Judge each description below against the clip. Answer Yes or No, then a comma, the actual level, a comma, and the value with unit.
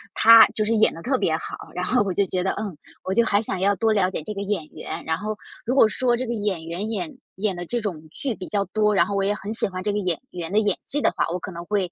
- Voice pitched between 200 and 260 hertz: Yes, high, 205 Hz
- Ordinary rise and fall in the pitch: Yes, average, 3.1 semitones